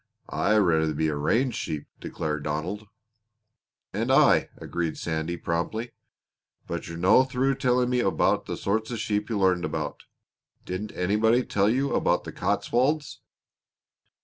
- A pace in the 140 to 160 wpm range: Yes, average, 145 wpm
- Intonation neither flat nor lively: No, wide, 6.6 semitones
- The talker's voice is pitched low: Yes, low, 105 Hz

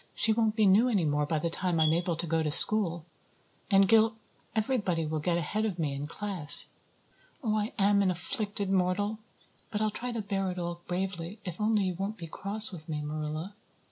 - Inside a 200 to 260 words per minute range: Yes, fast, 205 wpm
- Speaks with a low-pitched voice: No, high, 190 Hz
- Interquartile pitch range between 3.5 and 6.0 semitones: Yes, average, 4.3 semitones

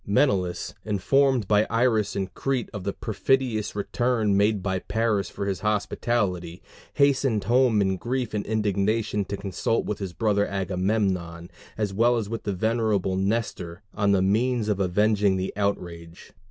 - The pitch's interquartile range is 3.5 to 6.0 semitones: No, average, 2.9 semitones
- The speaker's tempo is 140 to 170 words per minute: Yes, average, 155 wpm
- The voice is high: No, low, 105 Hz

